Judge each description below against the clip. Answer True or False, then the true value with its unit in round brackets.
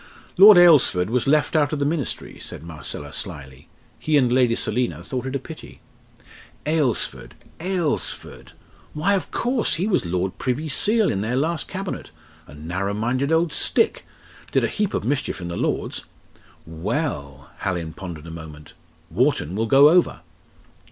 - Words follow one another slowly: False (160 wpm)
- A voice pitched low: True (125 Hz)